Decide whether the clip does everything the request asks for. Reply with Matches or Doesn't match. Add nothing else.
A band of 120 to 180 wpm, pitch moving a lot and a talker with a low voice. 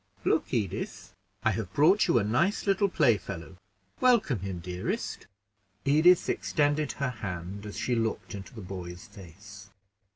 Matches